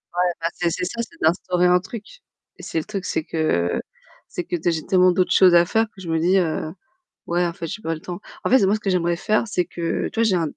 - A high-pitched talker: No, medium, 180 Hz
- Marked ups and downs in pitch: No, narrow, 2.6 semitones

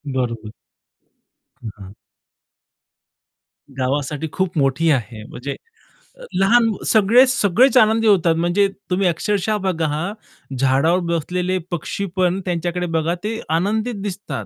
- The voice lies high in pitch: No, medium, 180 Hz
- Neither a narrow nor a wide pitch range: No, wide, 5.7 semitones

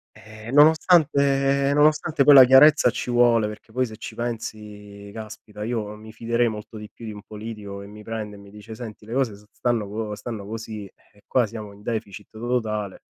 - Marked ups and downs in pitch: No, narrow, 2.6 semitones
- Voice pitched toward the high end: No, low, 110 Hz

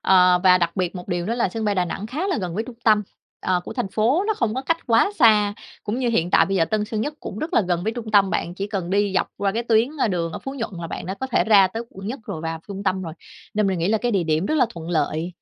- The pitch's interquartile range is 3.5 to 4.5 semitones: Yes, average, 4.1 semitones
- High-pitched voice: Yes, high, 200 Hz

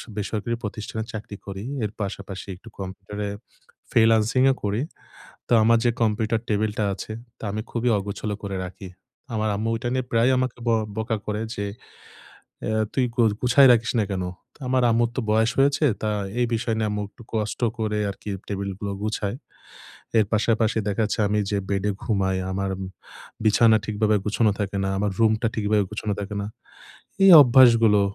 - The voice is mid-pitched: No, low, 110 Hz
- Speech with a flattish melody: Yes, narrow, 2.0 semitones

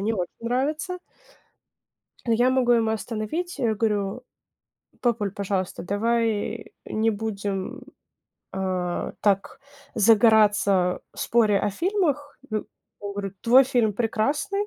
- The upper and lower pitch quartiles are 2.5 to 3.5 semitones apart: Yes, average, 3.2 semitones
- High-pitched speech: Yes, high, 220 Hz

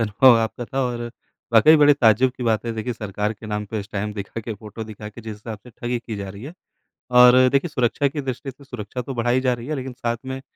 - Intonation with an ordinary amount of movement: Yes, average, 3.1 semitones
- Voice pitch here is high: No, low, 120 Hz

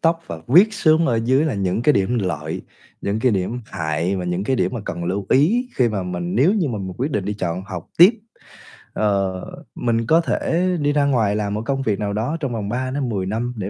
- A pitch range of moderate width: No, wide, 6.4 semitones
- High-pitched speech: No, low, 110 Hz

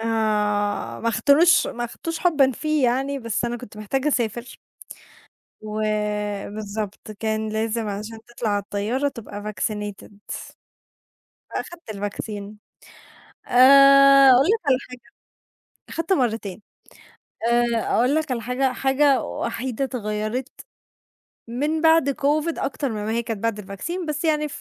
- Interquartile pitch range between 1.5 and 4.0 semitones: No, average, 4.5 semitones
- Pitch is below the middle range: No, high, 235 Hz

